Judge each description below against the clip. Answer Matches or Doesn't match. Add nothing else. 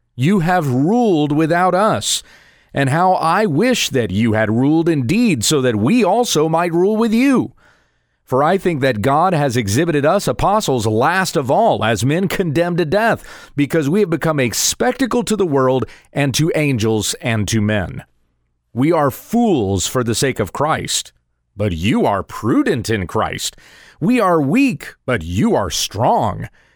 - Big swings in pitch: Matches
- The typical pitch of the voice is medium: Matches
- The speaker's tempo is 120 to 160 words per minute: Doesn't match